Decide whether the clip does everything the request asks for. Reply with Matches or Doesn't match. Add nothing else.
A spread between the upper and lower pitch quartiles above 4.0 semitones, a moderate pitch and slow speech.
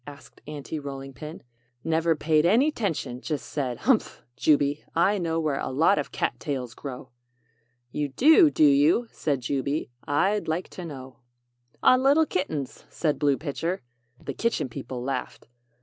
Doesn't match